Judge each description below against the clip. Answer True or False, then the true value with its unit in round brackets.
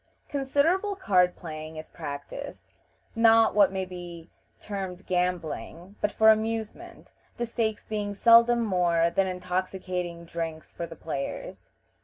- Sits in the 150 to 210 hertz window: True (185 Hz)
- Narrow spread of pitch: False (4.7 semitones)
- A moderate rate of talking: False (125 wpm)